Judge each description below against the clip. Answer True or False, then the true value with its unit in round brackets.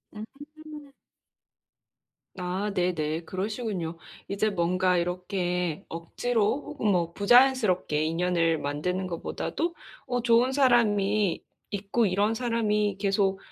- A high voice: True (200 Hz)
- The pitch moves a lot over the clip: False (4.6 semitones)